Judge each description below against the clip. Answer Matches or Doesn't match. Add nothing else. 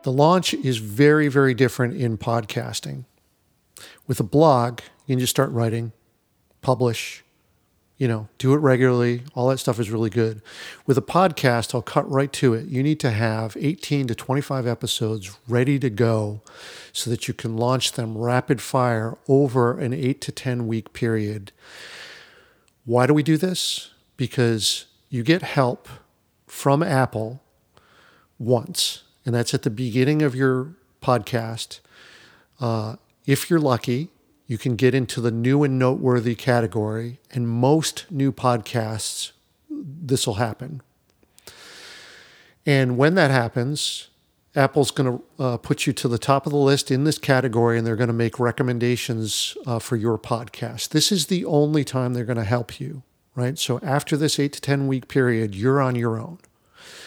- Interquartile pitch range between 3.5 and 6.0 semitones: Doesn't match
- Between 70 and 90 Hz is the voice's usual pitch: Doesn't match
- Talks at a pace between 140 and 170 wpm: Matches